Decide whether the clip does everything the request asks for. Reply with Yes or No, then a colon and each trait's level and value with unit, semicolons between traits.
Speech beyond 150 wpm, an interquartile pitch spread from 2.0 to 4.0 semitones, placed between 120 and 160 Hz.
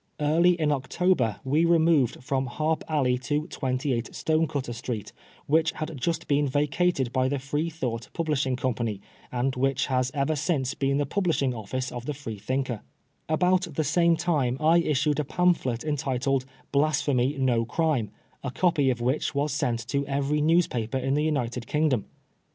Yes: average, 170 wpm; average, 3.5 semitones; medium, 140 Hz